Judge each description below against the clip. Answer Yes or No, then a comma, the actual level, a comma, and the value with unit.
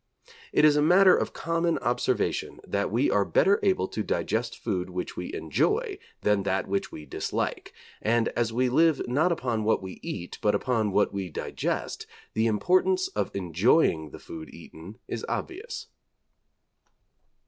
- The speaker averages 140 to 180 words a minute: Yes, average, 160 wpm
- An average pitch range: No, wide, 8.9 semitones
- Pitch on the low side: Yes, low, 115 Hz